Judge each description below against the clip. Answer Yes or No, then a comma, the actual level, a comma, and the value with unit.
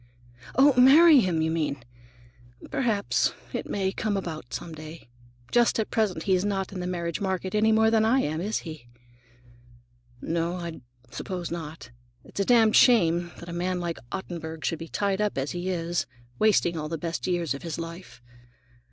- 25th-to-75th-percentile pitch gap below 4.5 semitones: Yes, average, 3.9 semitones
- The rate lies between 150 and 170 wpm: No, average, 180 wpm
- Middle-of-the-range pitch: Yes, medium, 175 Hz